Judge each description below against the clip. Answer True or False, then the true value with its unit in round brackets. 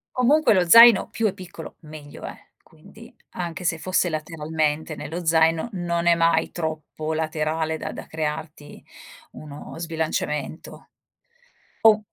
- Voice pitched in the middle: True (160 Hz)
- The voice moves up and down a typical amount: False (2.2 semitones)